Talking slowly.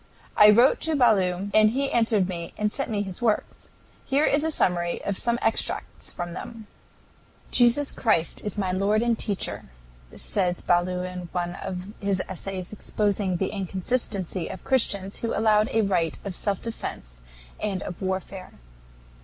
No: average, 160 wpm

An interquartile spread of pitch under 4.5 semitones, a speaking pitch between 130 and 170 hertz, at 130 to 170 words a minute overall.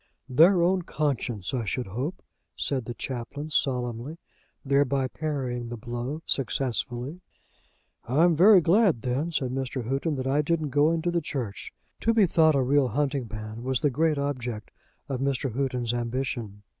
Yes: average, 4.0 semitones; low, 135 Hz; average, 160 wpm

